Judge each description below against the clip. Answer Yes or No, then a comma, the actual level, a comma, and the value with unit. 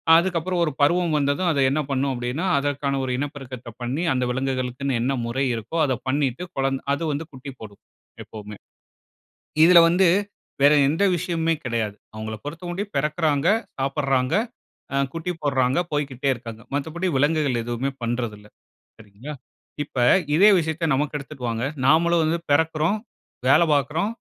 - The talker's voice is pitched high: No, medium, 140 Hz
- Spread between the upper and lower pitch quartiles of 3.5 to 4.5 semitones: Yes, average, 4.2 semitones